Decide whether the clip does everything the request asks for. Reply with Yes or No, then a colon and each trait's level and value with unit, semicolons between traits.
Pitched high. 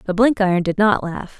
Yes: high, 200 Hz